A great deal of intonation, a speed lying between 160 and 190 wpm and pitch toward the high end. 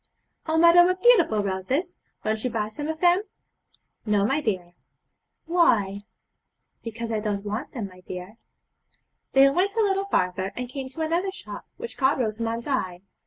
Yes: wide, 8.4 semitones; average, 165 wpm; high, 245 Hz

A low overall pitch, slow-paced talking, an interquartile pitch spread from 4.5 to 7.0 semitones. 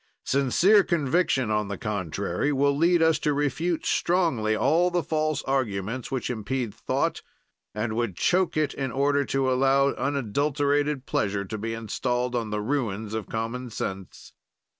No: low, 130 Hz; average, 150 wpm; average, 5.0 semitones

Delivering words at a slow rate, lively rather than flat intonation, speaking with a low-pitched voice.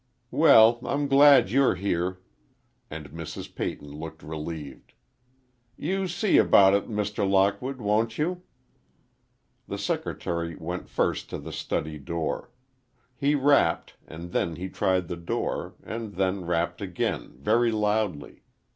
Yes: slow, 130 wpm; wide, 5.9 semitones; very low, 95 Hz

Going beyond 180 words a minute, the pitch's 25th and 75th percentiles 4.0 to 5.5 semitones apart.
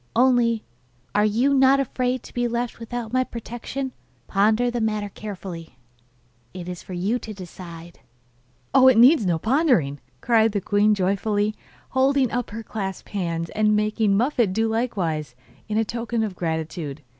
No: average, 155 wpm; average, 4.3 semitones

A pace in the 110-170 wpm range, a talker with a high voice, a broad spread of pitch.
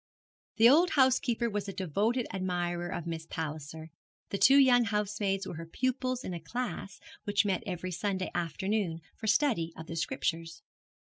Yes: average, 160 wpm; high, 195 Hz; wide, 5.7 semitones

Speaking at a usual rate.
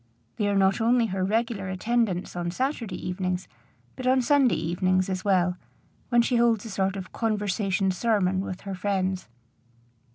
Yes: average, 160 wpm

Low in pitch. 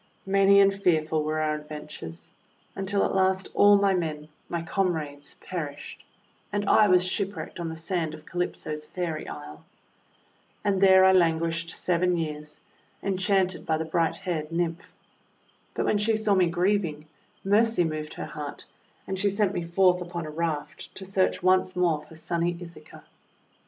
No: medium, 175 Hz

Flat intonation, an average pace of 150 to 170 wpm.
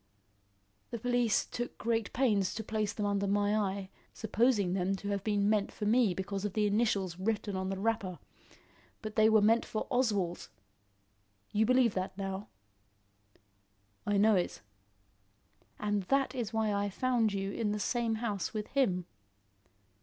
Yes: narrow, 2.3 semitones; average, 160 wpm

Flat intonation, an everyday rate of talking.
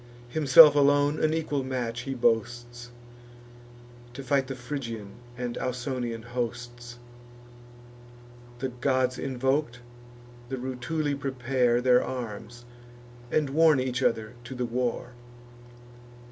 No: narrow, 2.1 semitones; slow, 105 wpm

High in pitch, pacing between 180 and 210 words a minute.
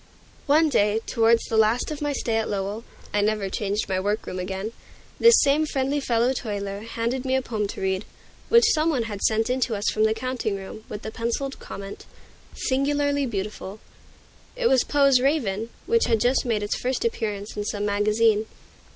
Yes: high, 225 Hz; average, 190 wpm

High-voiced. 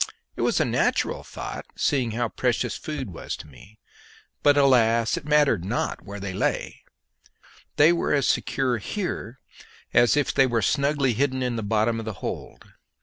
No: low, 120 Hz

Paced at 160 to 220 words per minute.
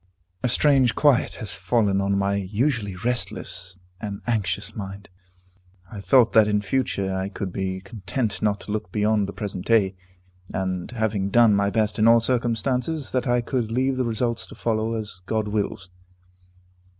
Yes: average, 165 wpm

